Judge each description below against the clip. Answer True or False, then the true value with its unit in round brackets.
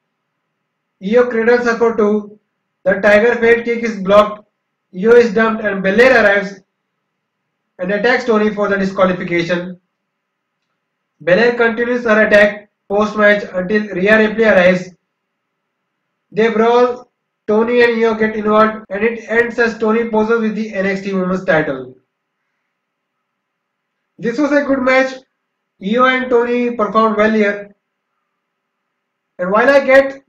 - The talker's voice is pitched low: False (215 Hz)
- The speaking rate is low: True (130 wpm)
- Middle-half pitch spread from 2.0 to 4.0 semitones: True (2.7 semitones)